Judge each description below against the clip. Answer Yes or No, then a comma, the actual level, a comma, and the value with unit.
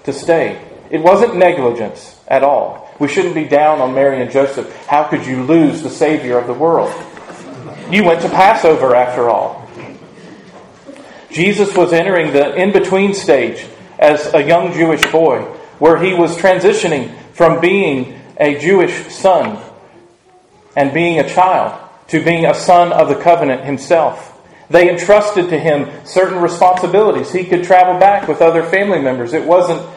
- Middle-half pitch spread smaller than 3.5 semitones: No, average, 3.8 semitones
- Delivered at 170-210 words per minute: No, average, 160 wpm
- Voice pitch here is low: No, medium, 170 Hz